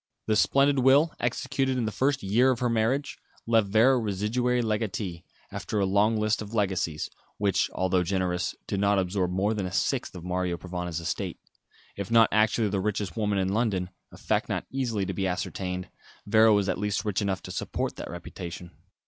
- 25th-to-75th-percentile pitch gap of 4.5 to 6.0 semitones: No, average, 3.5 semitones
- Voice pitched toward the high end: No, low, 105 Hz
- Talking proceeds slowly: No, average, 190 wpm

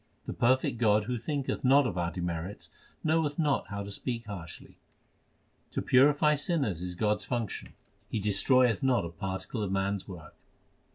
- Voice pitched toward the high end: No, low, 110 Hz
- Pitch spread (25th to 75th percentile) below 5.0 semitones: No, wide, 5.4 semitones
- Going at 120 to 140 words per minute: No, average, 170 wpm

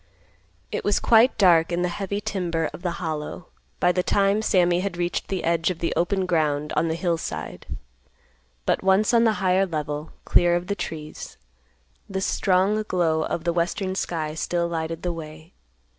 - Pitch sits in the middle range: Yes, medium, 175 Hz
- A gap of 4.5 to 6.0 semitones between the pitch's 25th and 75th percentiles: No, average, 2.8 semitones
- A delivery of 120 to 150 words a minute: No, average, 180 wpm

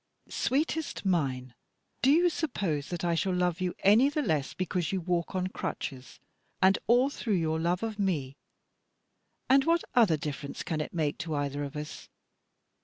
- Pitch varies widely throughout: Yes, wide, 6.6 semitones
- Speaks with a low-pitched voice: No, medium, 180 Hz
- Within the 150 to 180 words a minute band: Yes, average, 170 wpm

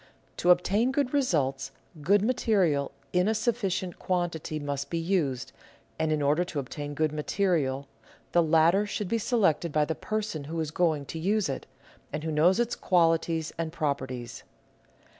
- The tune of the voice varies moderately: Yes, average, 4.7 semitones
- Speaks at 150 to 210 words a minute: Yes, average, 160 wpm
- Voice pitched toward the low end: No, medium, 165 Hz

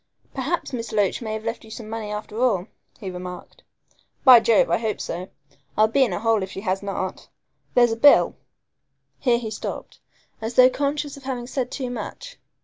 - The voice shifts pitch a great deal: No, average, 3.3 semitones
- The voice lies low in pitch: No, high, 225 Hz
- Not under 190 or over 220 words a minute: Yes, average, 200 wpm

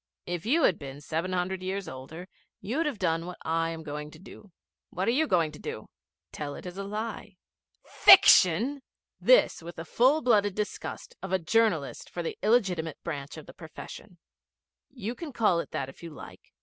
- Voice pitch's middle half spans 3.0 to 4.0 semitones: No, average, 5.1 semitones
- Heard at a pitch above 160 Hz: Yes, medium, 185 Hz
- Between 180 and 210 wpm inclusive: Yes, average, 190 wpm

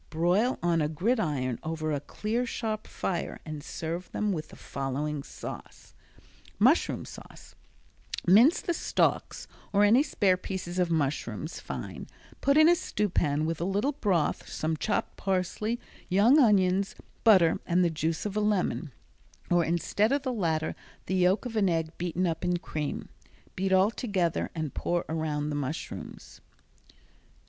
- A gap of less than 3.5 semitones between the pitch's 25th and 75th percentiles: No, average, 4.8 semitones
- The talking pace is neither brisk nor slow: Yes, average, 155 wpm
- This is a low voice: No, medium, 180 Hz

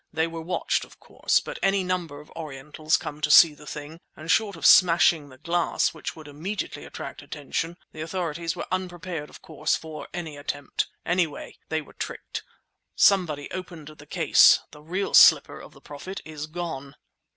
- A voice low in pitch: No, medium, 160 Hz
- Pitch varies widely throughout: No, average, 2.8 semitones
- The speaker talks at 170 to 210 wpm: Yes, average, 175 wpm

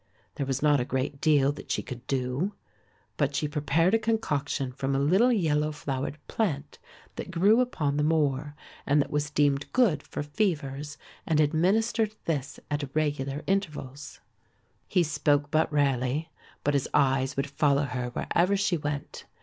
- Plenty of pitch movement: No, average, 2.8 semitones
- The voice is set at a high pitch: No, medium, 145 Hz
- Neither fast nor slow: Yes, average, 160 wpm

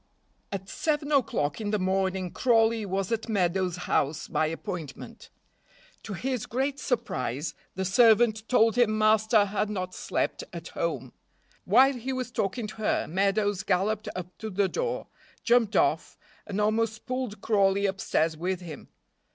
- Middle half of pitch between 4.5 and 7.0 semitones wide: No, average, 3.6 semitones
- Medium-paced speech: Yes, average, 150 wpm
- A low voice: No, high, 210 Hz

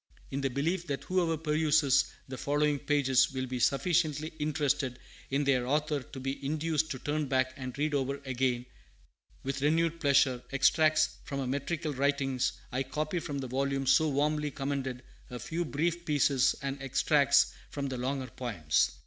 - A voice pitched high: No, medium, 140 Hz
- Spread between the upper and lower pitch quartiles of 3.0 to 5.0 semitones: No, narrow, 2.4 semitones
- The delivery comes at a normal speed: Yes, average, 165 wpm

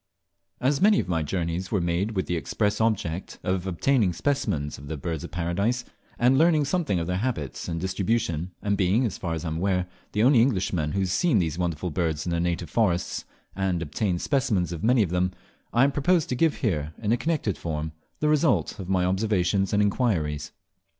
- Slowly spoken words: No, fast, 205 wpm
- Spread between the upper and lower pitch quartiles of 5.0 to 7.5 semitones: Yes, wide, 5.5 semitones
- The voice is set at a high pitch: No, very low, 95 Hz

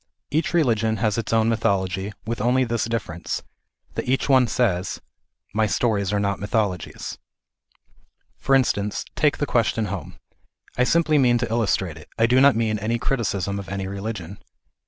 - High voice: No, low, 110 Hz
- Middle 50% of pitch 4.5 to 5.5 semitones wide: No, average, 3.4 semitones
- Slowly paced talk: No, average, 165 wpm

